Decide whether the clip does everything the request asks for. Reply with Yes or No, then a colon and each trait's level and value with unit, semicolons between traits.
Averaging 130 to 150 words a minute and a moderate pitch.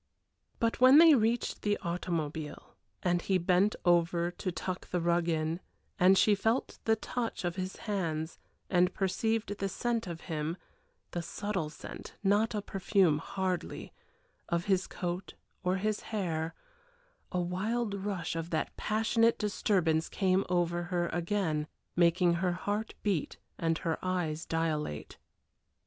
Yes: average, 140 wpm; medium, 180 Hz